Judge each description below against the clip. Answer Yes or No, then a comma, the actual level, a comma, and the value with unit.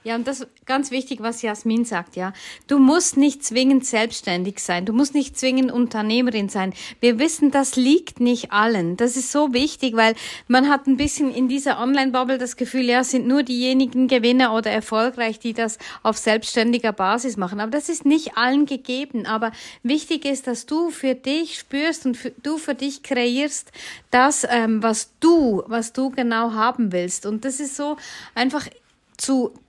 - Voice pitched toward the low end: No, very high, 255 Hz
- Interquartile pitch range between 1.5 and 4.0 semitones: Yes, average, 3.3 semitones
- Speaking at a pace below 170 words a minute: No, average, 185 wpm